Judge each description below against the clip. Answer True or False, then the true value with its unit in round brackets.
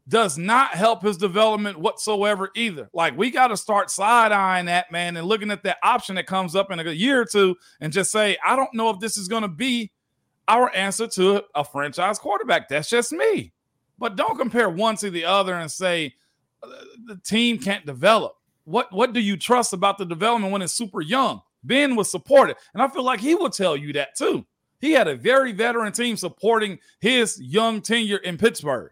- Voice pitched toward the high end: True (210 Hz)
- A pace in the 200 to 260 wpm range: True (205 wpm)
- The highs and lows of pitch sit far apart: False (3.7 semitones)